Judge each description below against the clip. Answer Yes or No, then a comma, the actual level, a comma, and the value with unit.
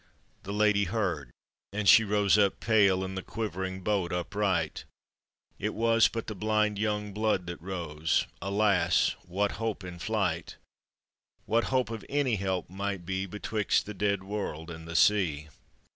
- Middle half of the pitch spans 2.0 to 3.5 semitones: Yes, average, 2.9 semitones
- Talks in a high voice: No, low, 100 Hz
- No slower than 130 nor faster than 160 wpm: Yes, average, 155 wpm